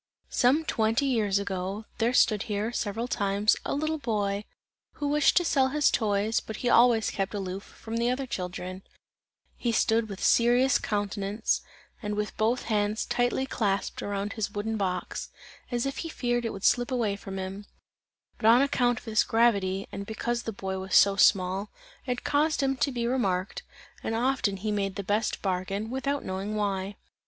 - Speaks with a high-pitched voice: Yes, high, 215 Hz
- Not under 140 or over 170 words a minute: No, average, 180 wpm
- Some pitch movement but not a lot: Yes, average, 3.5 semitones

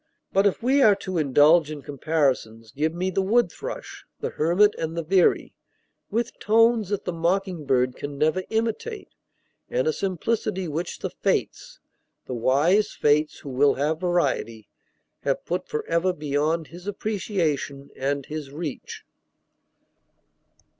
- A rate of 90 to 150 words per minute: Yes, average, 140 wpm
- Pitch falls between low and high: Yes, medium, 170 Hz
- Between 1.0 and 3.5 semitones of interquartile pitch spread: No, wide, 5.5 semitones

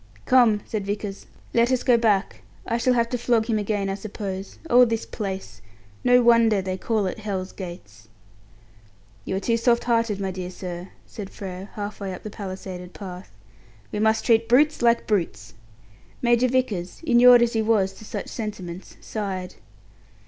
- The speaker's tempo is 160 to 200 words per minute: Yes, average, 170 wpm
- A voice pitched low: No, high, 210 Hz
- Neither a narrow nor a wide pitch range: Yes, average, 3.6 semitones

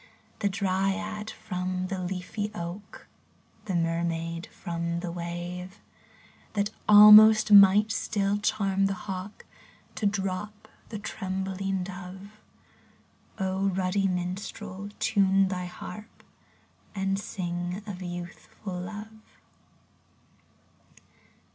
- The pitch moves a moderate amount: No, narrow, 2.2 semitones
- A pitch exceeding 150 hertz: Yes, high, 190 Hz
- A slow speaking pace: Yes, slow, 90 wpm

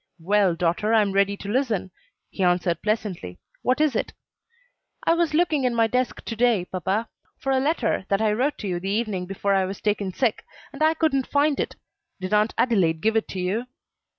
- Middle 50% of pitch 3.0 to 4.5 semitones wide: No, average, 5.0 semitones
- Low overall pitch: No, high, 210 Hz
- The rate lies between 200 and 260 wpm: Yes, fast, 205 wpm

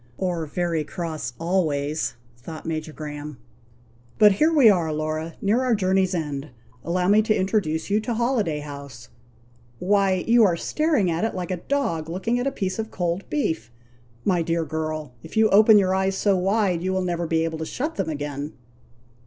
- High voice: No, medium, 180 Hz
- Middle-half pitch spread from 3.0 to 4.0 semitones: No, average, 4.7 semitones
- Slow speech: No, average, 185 wpm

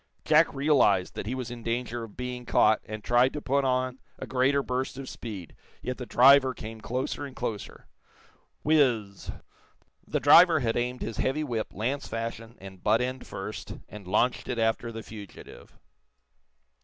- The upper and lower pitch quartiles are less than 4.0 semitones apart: Yes, average, 2.8 semitones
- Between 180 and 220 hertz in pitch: No, low, 120 Hz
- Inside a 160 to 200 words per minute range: Yes, average, 170 wpm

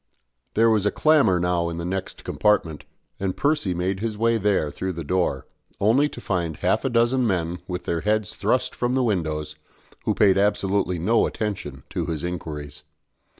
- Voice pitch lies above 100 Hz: No, very low, 95 Hz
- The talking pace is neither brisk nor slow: Yes, average, 180 wpm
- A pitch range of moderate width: Yes, average, 4.2 semitones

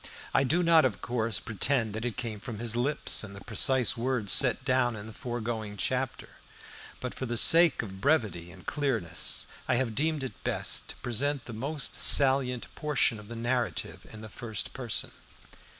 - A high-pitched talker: No, low, 120 Hz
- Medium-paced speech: Yes, average, 180 wpm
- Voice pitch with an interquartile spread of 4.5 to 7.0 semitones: No, average, 3.4 semitones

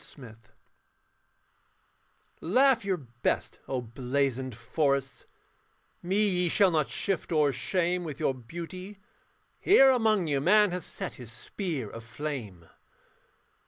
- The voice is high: No, medium, 155 Hz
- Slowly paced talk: Yes, slow, 125 wpm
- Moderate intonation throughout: No, wide, 6.8 semitones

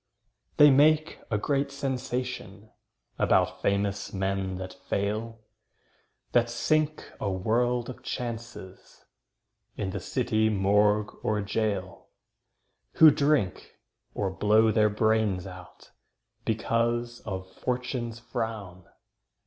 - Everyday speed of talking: No, slow, 100 wpm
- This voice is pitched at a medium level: No, low, 110 Hz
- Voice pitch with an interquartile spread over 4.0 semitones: No, average, 3.4 semitones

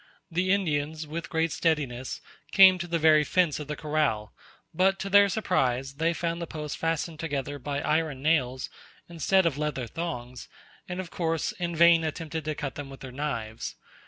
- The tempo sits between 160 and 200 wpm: Yes, average, 180 wpm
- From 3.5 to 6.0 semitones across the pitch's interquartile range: No, average, 3.1 semitones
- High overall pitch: No, medium, 155 Hz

